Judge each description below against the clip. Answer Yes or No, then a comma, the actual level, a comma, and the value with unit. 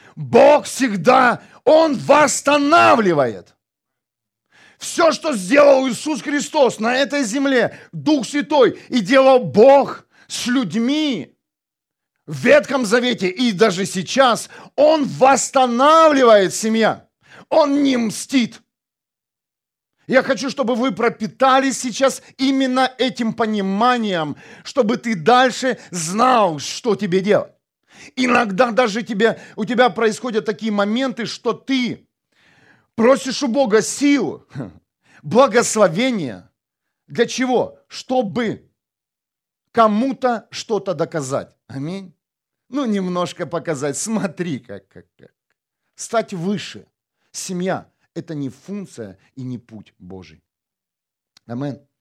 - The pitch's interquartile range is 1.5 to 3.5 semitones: No, average, 5.3 semitones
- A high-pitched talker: Yes, high, 240 Hz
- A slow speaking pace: Yes, slow, 100 wpm